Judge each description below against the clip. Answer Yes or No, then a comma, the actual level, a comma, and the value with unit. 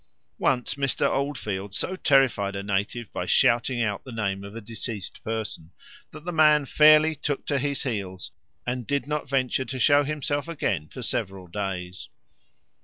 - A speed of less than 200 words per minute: Yes, average, 165 wpm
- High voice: No, low, 120 Hz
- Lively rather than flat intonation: Yes, wide, 6.1 semitones